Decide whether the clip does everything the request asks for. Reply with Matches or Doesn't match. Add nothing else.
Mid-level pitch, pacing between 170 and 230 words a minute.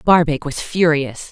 Doesn't match